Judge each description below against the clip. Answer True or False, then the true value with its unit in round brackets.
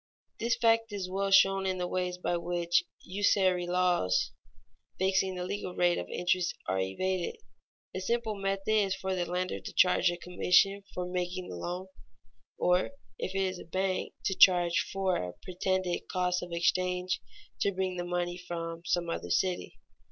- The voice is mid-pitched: True (180 Hz)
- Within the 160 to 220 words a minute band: True (175 wpm)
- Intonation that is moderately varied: False (1.4 semitones)